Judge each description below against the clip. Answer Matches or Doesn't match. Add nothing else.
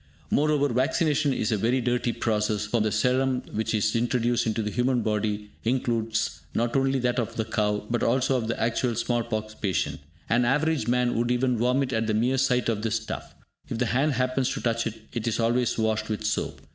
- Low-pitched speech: Matches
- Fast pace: Matches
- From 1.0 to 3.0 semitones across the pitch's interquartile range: Matches